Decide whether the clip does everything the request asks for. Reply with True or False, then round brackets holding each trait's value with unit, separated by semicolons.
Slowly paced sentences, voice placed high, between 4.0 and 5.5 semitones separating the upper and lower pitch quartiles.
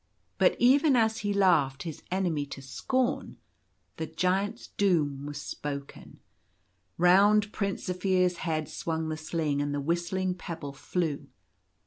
False (130 wpm; 175 Hz; 4.8 semitones)